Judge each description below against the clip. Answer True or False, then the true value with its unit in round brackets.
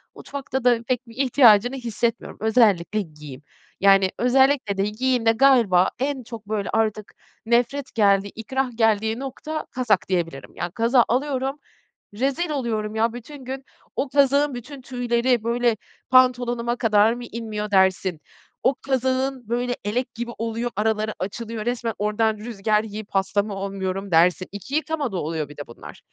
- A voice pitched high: True (230 Hz)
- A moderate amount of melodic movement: True (3.6 semitones)